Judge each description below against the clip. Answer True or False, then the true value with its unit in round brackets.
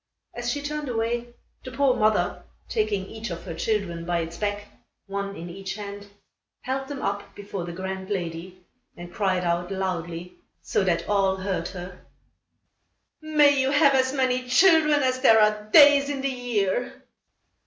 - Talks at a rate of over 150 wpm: True (165 wpm)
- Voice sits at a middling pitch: False (205 Hz)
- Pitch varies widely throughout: True (5.7 semitones)